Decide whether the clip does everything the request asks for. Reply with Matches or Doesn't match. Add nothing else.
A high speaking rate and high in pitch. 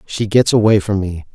Doesn't match